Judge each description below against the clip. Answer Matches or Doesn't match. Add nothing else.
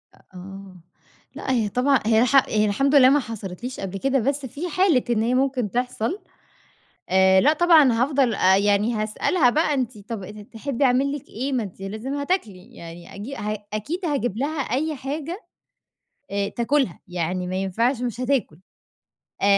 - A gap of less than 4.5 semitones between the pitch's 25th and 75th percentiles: Doesn't match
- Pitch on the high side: Matches